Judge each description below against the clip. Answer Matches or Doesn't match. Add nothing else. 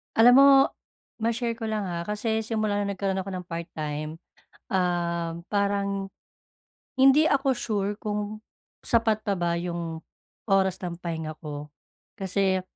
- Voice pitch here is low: Doesn't match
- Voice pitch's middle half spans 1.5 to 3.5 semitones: Doesn't match